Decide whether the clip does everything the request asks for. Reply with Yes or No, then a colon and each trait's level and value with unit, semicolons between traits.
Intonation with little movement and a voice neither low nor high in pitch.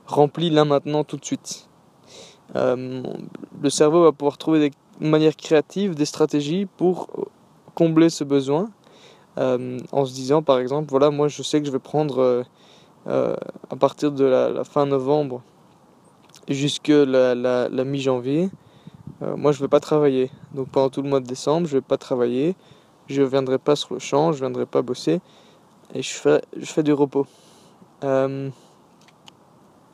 Yes: narrow, 2.2 semitones; medium, 145 Hz